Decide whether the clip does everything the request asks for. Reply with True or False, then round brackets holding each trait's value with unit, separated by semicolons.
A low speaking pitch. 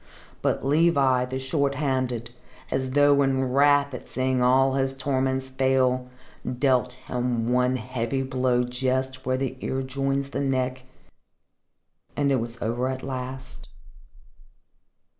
True (130 Hz)